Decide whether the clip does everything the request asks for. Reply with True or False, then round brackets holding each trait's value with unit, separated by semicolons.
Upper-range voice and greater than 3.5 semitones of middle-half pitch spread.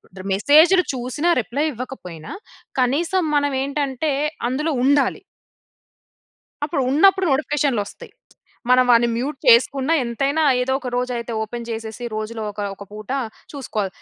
True (260 Hz; 4.0 semitones)